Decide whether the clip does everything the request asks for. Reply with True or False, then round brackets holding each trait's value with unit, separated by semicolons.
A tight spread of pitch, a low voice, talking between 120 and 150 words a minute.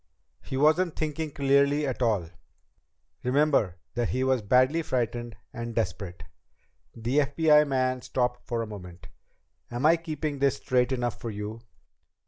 False (3.8 semitones; 130 Hz; 140 wpm)